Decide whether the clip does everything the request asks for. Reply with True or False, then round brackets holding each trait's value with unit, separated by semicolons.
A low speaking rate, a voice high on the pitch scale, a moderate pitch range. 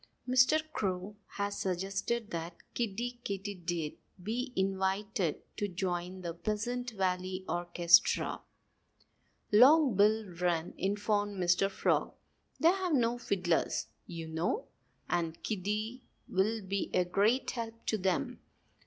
True (115 wpm; 200 Hz; 3.9 semitones)